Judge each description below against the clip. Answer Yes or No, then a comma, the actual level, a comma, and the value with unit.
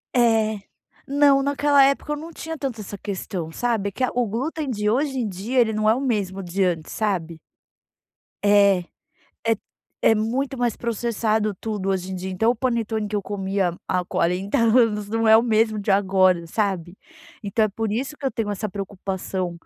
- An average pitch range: Yes, average, 3.6 semitones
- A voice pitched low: No, high, 215 Hz